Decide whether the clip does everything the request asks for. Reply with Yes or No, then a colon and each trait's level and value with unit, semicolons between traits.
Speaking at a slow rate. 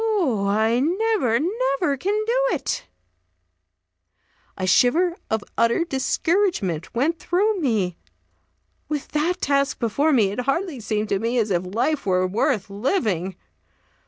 Yes: slow, 130 wpm